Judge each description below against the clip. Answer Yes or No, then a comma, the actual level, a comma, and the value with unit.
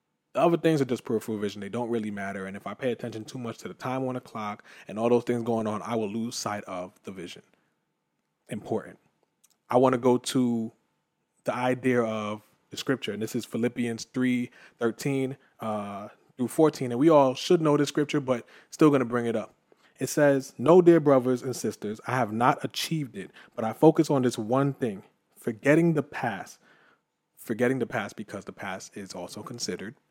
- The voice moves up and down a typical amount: Yes, average, 3.4 semitones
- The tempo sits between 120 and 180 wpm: No, fast, 205 wpm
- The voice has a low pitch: Yes, low, 125 Hz